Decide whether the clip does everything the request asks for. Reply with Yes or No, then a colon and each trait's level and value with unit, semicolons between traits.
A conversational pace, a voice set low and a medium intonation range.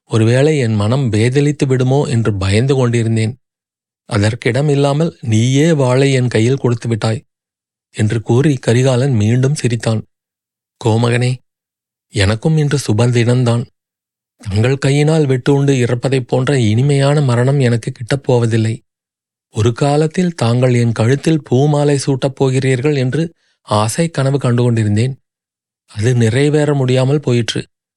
Yes: average, 110 wpm; low, 130 Hz; average, 3.3 semitones